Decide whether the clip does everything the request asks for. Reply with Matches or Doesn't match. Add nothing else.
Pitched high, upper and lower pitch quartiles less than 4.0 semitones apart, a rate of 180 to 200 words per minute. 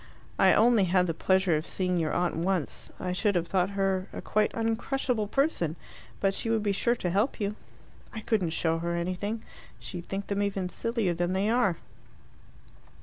Matches